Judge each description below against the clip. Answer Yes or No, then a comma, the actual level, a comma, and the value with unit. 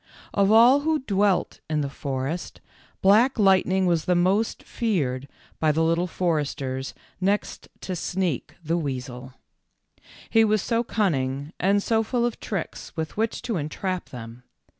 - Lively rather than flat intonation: Yes, wide, 6.4 semitones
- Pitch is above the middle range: No, medium, 180 Hz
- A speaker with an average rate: Yes, average, 150 wpm